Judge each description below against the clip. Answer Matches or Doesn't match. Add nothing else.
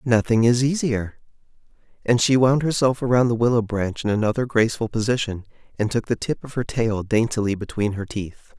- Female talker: Doesn't match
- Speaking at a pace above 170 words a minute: Matches